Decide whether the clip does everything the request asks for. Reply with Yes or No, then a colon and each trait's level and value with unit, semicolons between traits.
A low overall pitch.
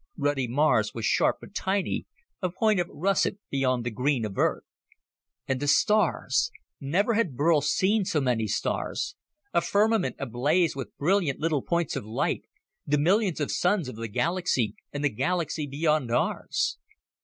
No: medium, 150 Hz